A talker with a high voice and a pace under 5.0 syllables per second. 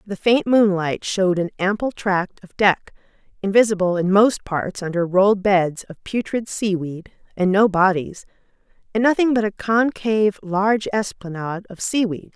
Yes: high, 200 Hz; 4.7 syllables/s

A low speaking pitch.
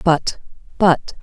No: medium, 170 Hz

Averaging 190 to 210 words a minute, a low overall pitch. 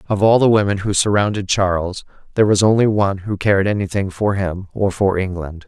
Yes: average, 200 wpm; low, 100 Hz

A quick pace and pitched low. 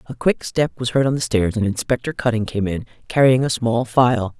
Yes: fast, 230 wpm; low, 120 Hz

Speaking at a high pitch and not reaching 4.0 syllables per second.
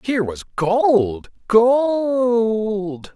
Yes: high, 215 Hz; 1.8 syllables/s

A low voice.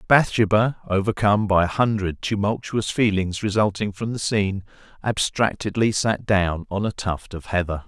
Yes: low, 100 Hz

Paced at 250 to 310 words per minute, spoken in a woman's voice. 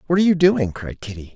No: fast, 265 wpm; male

